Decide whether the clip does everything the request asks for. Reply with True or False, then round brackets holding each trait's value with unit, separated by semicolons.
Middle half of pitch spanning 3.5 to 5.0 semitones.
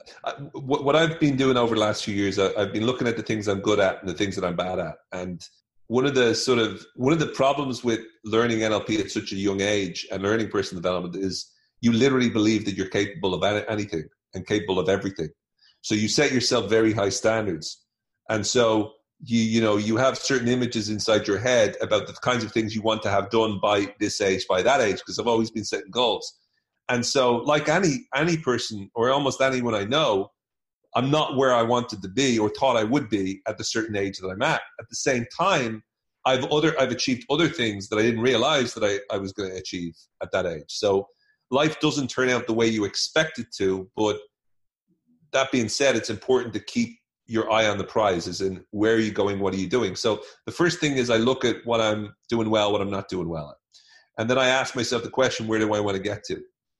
True (3.9 semitones)